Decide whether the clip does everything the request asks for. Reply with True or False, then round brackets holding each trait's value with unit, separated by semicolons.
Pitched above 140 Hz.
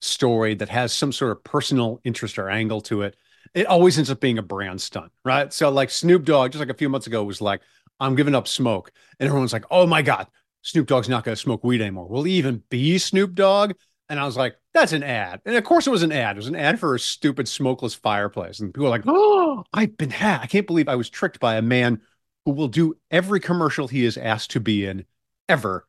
False (135 Hz)